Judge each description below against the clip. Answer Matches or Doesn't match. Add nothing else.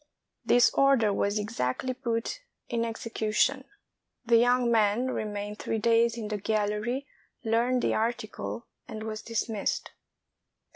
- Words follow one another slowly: Matches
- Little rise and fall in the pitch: Matches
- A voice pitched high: Matches